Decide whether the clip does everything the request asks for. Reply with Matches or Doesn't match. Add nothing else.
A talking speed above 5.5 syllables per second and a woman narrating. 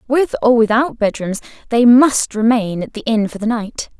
Doesn't match